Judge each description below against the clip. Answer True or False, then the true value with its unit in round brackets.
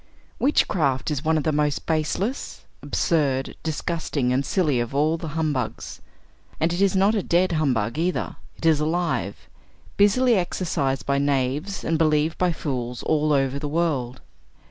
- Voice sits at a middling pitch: True (155 Hz)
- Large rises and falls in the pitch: False (3.7 semitones)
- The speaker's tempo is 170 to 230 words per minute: False (155 wpm)